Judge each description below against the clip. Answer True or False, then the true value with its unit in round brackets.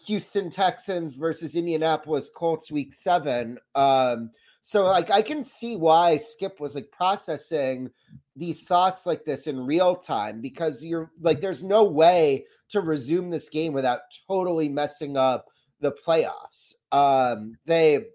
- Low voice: False (165 Hz)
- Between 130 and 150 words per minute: True (140 wpm)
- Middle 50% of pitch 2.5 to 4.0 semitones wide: False (4.6 semitones)